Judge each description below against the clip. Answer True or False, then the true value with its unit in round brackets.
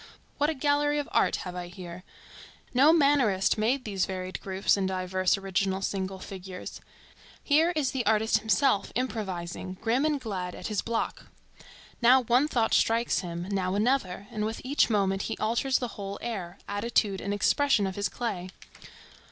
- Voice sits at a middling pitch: False (210 Hz)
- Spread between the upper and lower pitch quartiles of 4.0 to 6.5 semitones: True (4.9 semitones)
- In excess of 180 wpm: False (165 wpm)